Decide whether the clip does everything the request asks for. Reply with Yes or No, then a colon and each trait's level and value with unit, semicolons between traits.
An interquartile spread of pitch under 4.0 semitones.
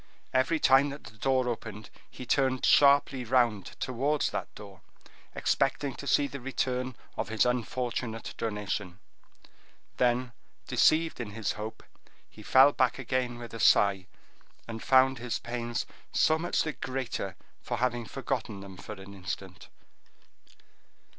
Yes: average, 3.4 semitones